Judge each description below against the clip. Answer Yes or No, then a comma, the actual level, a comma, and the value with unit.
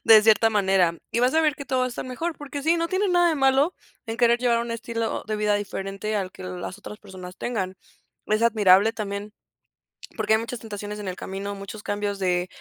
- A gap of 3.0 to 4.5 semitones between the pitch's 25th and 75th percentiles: Yes, average, 3.7 semitones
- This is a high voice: Yes, high, 215 Hz